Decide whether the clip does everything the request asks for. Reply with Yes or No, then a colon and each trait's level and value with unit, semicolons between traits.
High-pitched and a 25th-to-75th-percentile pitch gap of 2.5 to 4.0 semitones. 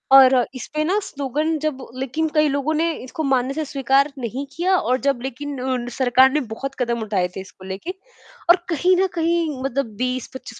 Yes: very high, 270 Hz; average, 3.4 semitones